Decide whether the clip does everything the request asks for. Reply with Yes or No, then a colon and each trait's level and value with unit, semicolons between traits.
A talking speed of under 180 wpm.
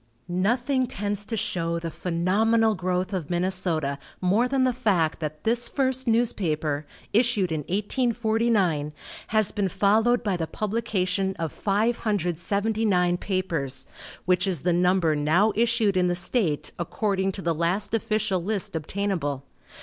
Yes: slow, 135 wpm